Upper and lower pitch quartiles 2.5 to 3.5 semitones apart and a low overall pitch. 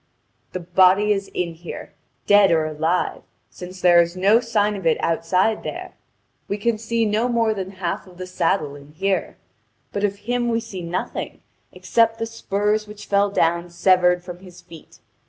No: average, 3.1 semitones; high, 190 Hz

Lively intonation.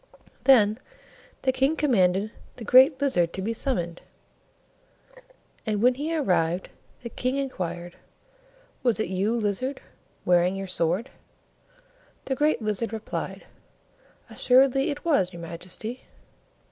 Yes: wide, 6.3 semitones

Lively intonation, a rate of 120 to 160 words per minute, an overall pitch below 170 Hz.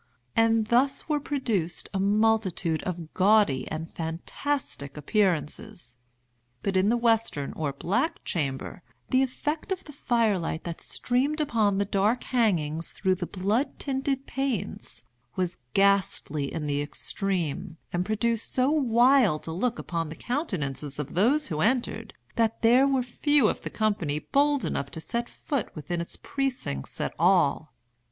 No: wide, 7.1 semitones; average, 150 wpm; high, 205 Hz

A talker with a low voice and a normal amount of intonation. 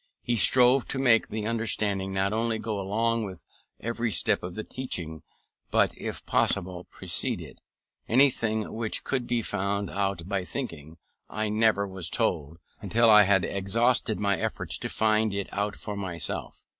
Yes: low, 105 Hz; average, 3.1 semitones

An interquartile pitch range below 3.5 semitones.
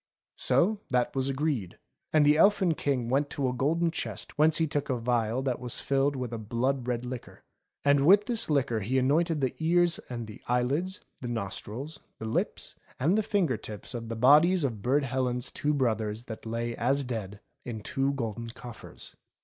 No: average, 4.1 semitones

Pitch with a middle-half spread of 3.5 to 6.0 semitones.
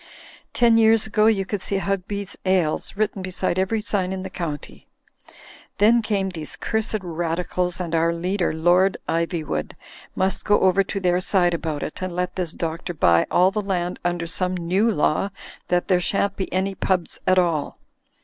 No: narrow, 2.4 semitones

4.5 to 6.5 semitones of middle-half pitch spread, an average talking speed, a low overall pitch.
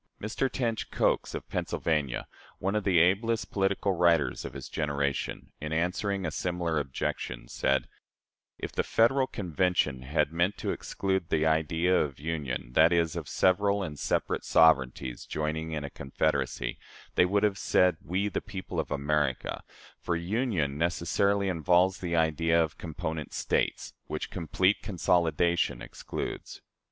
No: average, 3.8 semitones; average, 145 wpm; very low, 85 Hz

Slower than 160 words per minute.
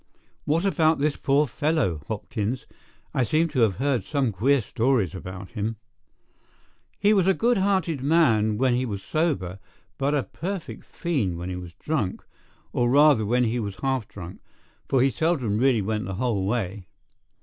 No: average, 170 wpm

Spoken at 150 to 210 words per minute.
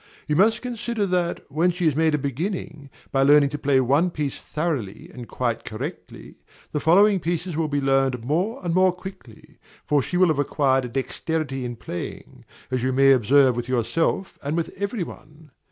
Yes: average, 185 wpm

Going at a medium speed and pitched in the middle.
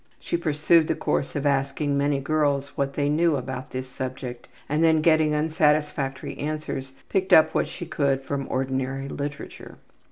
Yes: average, 160 wpm; medium, 145 Hz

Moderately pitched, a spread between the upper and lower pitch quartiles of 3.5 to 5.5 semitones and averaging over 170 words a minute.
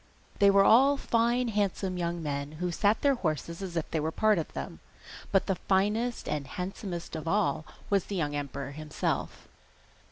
Yes: medium, 180 Hz; average, 4.9 semitones; average, 180 wpm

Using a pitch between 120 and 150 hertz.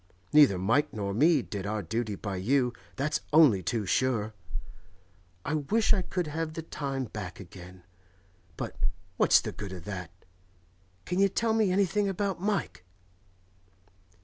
Yes: low, 135 Hz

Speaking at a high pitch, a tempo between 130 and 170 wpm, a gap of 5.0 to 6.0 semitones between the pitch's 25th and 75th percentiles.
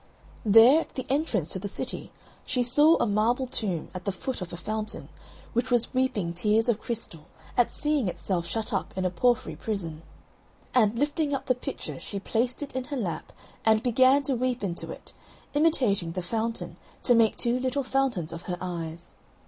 No: high, 225 Hz; average, 190 wpm; wide, 5.5 semitones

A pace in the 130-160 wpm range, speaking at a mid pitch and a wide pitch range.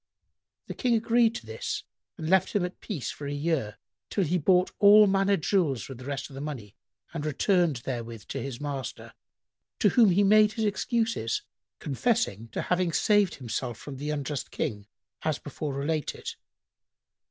No: average, 170 wpm; medium, 155 Hz; wide, 6.9 semitones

